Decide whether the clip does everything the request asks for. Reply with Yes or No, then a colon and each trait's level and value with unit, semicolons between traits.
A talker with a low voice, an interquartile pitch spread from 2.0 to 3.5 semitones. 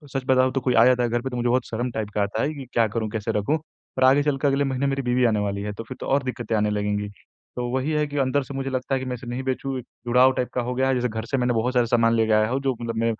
Yes: low, 125 Hz; average, 2.7 semitones